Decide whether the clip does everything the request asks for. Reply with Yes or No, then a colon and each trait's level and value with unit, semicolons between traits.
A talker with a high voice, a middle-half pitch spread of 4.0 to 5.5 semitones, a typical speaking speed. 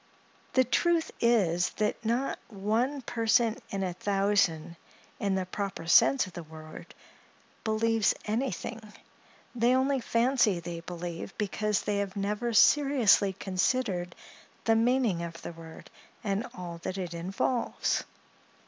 No: high, 205 Hz; average, 4.8 semitones; slow, 130 wpm